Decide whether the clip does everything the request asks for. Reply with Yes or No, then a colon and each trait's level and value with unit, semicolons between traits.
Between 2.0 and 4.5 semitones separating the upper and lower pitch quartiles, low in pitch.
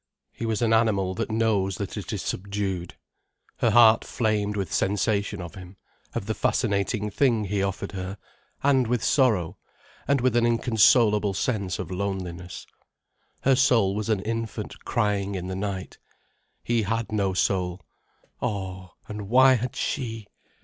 Yes: average, 3.0 semitones; low, 105 Hz